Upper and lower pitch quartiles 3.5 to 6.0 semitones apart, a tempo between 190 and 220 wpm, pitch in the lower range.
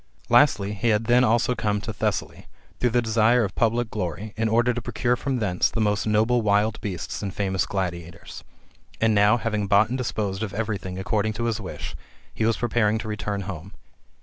No: narrow, 2.5 semitones; average, 200 wpm; low, 110 Hz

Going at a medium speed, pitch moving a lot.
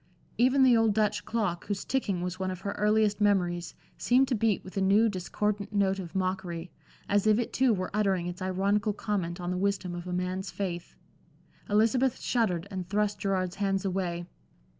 No: average, 185 wpm; narrow, 2.6 semitones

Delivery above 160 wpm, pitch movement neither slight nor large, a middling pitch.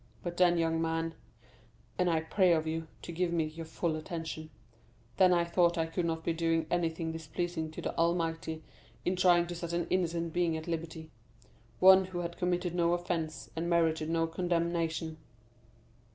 No: average, 170 wpm; narrow, 1.3 semitones; medium, 170 Hz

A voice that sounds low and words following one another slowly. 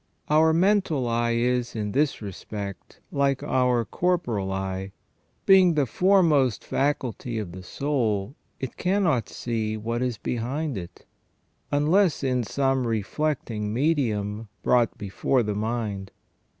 Yes: low, 120 Hz; slow, 125 wpm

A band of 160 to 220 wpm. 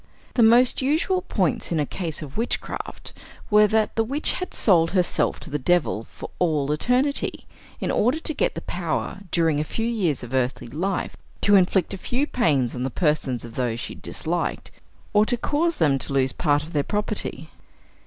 Yes: average, 190 wpm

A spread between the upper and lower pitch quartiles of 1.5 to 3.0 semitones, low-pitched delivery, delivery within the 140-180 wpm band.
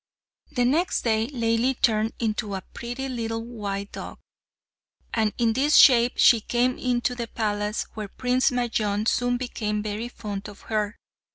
No: narrow, 2.5 semitones; high, 230 Hz; average, 150 wpm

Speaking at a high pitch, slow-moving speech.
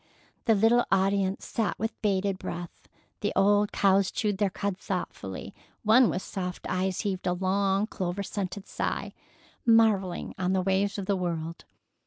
No: high, 195 Hz; average, 155 wpm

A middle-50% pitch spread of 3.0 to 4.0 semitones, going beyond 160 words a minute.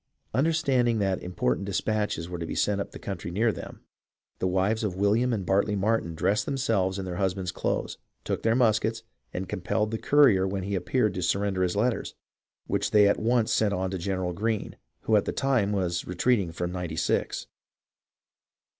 Yes: average, 3.3 semitones; average, 190 wpm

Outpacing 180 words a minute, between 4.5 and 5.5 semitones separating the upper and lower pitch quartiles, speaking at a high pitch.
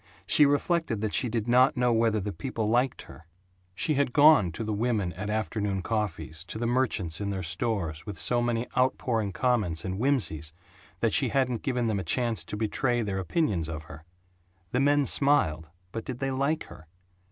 No: average, 190 wpm; average, 5.0 semitones; low, 110 Hz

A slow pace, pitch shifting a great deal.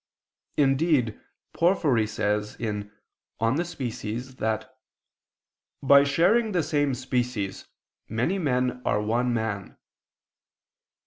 No: slow, 90 wpm; average, 4.7 semitones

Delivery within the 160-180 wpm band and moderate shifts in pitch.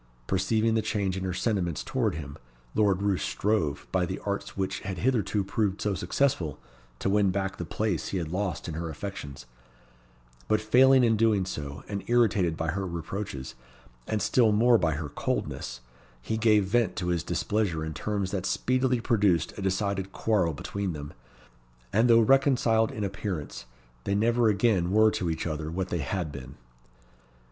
Yes: average, 170 wpm; average, 4.2 semitones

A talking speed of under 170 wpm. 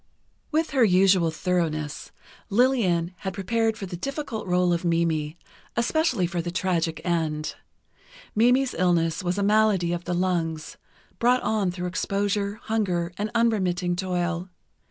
Yes: slow, 135 wpm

